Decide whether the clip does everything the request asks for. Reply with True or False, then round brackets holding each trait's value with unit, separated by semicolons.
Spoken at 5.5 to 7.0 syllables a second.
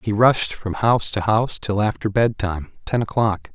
False (5.1 syllables/s)